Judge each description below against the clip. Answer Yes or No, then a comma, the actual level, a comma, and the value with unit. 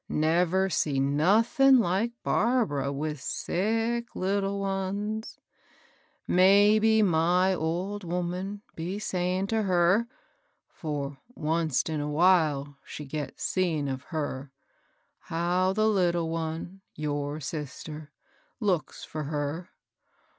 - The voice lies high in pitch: No, medium, 175 Hz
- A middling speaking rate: No, slow, 120 wpm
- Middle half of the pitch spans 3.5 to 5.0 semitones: Yes, average, 4.6 semitones